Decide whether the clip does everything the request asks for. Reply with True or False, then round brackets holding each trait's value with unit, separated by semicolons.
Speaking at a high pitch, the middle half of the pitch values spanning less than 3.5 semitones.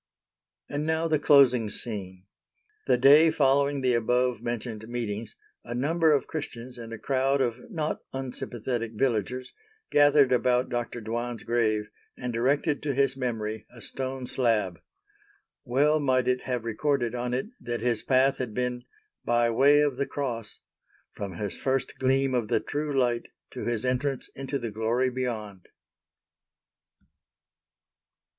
False (125 Hz; 2.7 semitones)